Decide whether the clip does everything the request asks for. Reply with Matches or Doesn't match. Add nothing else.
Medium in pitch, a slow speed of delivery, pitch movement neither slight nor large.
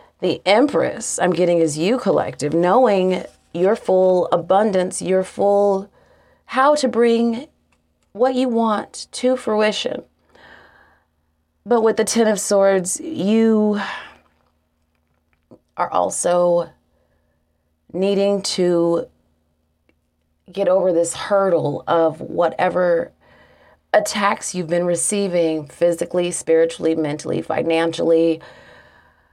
Matches